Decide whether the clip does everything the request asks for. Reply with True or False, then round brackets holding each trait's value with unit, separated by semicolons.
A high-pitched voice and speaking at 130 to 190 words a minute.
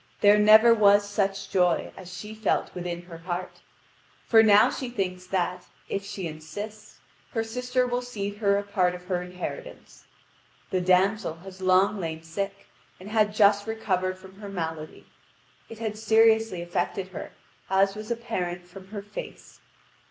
True (195 Hz; 160 wpm)